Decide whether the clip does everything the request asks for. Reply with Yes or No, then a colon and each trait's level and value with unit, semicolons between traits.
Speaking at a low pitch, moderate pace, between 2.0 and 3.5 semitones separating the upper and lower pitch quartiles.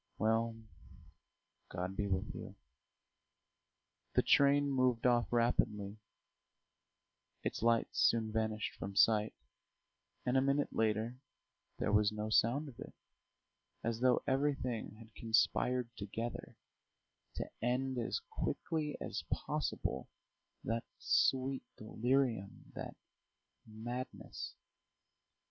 No: low, 115 Hz; slow, 100 wpm; average, 2.9 semitones